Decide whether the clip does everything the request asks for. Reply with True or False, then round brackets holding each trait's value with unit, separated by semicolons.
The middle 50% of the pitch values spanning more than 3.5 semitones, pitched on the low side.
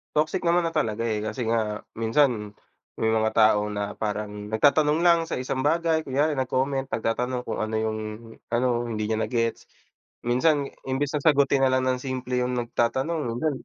True (4.4 semitones; 125 Hz)